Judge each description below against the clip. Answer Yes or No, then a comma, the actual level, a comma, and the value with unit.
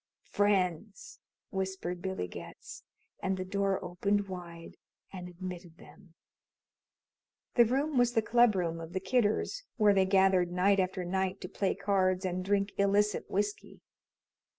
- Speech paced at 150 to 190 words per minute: No, average, 140 wpm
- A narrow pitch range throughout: Yes, narrow, 2.1 semitones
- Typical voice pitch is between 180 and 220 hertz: Yes, high, 190 Hz